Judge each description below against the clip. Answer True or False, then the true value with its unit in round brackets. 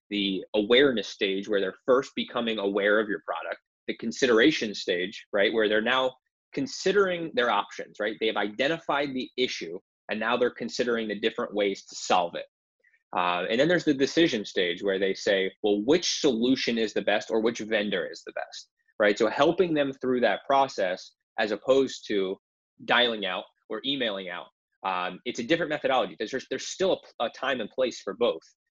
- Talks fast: False (190 wpm)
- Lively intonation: True (7.7 semitones)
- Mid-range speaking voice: False (125 Hz)